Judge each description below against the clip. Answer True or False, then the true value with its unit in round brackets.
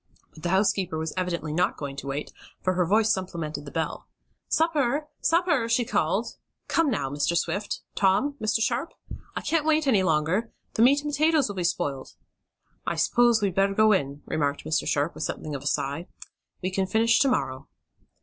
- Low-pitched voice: False (190 Hz)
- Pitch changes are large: True (7.2 semitones)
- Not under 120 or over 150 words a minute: False (190 wpm)